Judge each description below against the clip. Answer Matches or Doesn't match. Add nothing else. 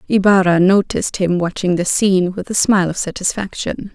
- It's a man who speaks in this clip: Doesn't match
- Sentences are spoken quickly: Doesn't match